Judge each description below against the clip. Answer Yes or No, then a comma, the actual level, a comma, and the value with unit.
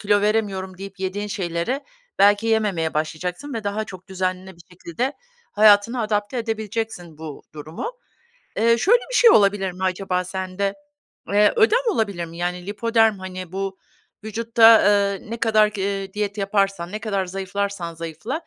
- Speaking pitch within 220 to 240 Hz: No, high, 200 Hz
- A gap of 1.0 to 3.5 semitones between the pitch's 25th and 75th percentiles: Yes, average, 2.9 semitones